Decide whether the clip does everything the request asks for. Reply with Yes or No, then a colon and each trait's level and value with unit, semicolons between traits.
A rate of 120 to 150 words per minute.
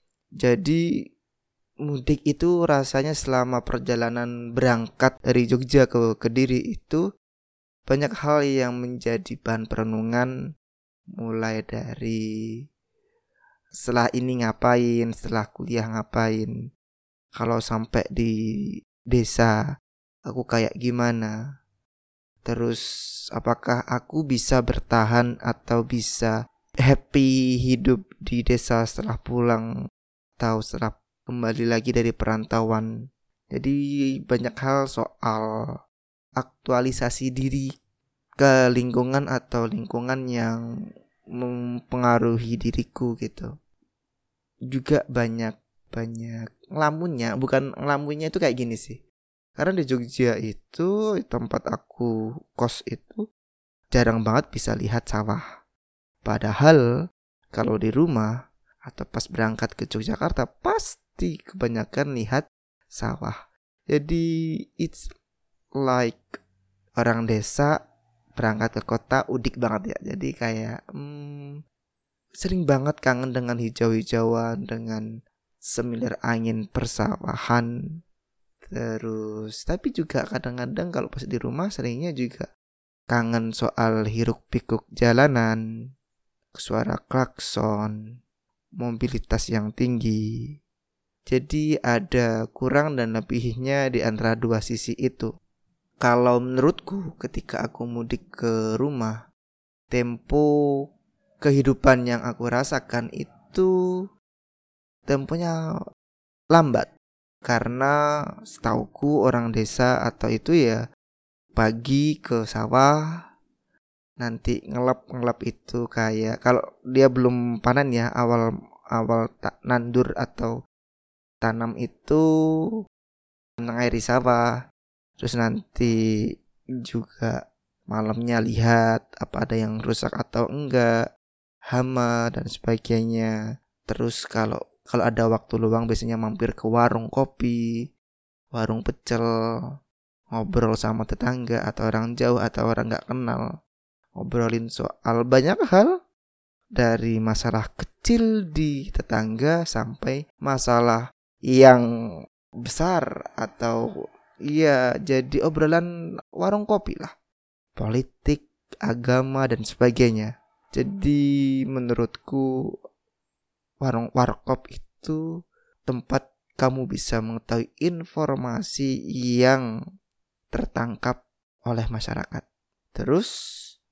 No: average, 95 wpm